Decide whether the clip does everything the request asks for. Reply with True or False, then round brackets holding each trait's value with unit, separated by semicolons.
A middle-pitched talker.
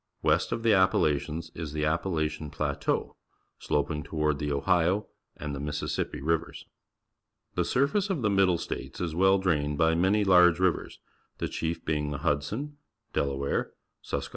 False (80 Hz)